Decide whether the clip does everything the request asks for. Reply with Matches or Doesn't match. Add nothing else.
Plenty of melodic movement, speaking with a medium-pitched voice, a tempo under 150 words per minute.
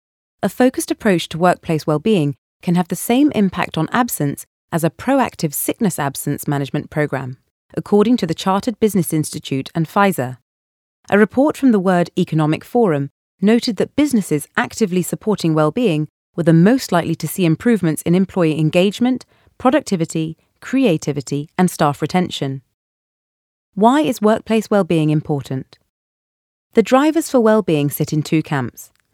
Matches